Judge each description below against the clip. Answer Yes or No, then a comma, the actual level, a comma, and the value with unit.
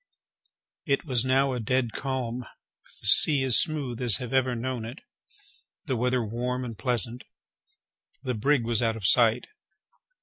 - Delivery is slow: No, average, 160 wpm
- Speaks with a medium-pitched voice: No, low, 125 Hz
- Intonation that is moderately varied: No, narrow, 2.2 semitones